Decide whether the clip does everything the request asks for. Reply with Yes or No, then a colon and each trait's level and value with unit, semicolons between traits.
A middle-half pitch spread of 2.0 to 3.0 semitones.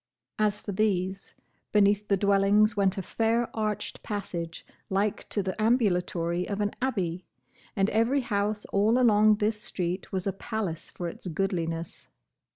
Yes: narrow, 2.5 semitones